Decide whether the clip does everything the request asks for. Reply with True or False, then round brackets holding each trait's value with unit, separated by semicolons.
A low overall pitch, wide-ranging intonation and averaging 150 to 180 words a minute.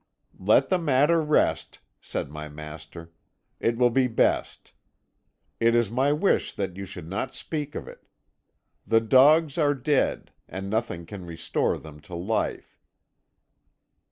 False (115 Hz; 8.2 semitones; 140 wpm)